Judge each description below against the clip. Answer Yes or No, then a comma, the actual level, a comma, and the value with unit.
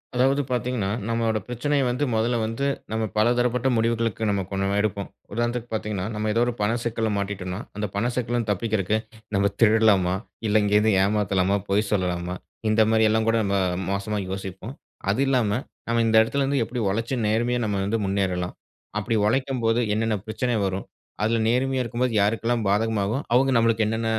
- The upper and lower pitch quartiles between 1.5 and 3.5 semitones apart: Yes, average, 2.8 semitones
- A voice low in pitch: Yes, low, 110 Hz